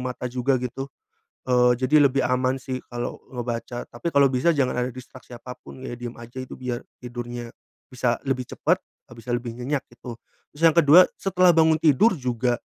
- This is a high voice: No, low, 125 Hz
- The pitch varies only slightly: Yes, narrow, 2.2 semitones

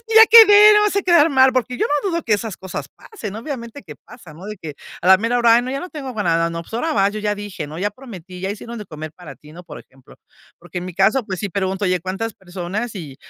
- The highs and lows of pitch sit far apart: Yes, wide, 6.1 semitones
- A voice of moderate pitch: No, high, 205 Hz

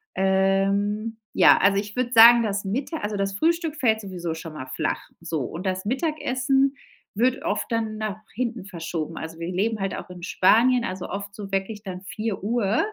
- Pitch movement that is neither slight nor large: Yes, average, 3.7 semitones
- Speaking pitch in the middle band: No, high, 205 Hz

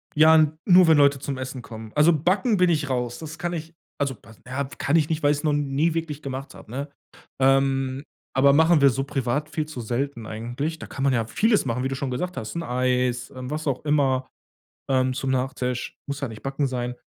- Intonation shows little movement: No, average, 3.2 semitones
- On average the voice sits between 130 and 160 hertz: Yes, medium, 140 Hz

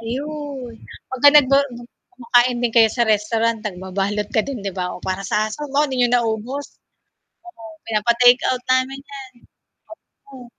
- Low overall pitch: No, high, 240 Hz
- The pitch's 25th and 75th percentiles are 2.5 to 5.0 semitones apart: Yes, average, 3.6 semitones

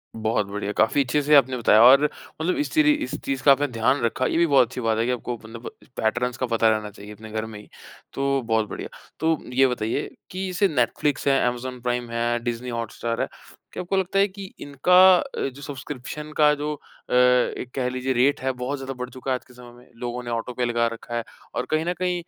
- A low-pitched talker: Yes, low, 125 Hz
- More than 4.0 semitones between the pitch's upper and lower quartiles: No, average, 3.5 semitones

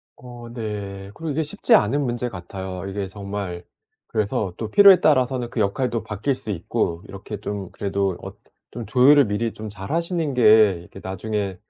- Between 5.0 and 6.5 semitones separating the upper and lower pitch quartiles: No, average, 4.2 semitones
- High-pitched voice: No, low, 105 Hz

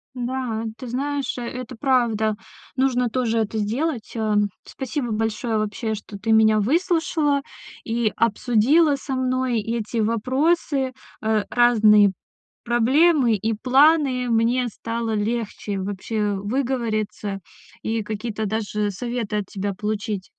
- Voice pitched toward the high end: Yes, high, 230 Hz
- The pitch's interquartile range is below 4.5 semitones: Yes, average, 3.2 semitones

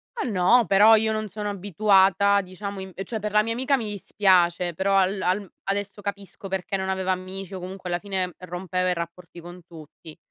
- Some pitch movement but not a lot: No, narrow, 2.0 semitones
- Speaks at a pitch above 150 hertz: Yes, high, 190 Hz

